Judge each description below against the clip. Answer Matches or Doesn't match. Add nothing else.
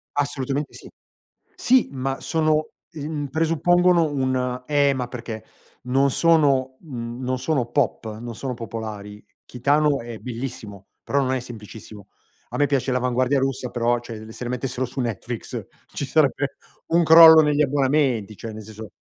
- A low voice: Matches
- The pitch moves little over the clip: Doesn't match